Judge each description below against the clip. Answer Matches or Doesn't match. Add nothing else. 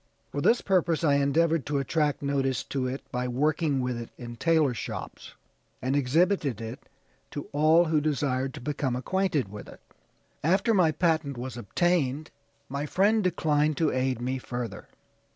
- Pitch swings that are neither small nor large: Matches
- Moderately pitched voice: Matches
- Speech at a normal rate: Matches